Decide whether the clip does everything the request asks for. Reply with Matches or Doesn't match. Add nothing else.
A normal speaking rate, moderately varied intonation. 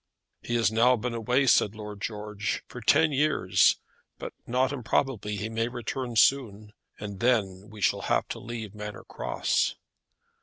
Matches